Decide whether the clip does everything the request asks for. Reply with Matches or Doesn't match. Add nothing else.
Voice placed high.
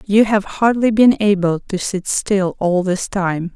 Matches